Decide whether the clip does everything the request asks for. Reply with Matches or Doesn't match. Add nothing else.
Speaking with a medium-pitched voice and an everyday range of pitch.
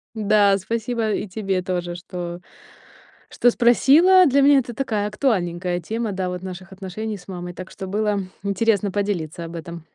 Doesn't match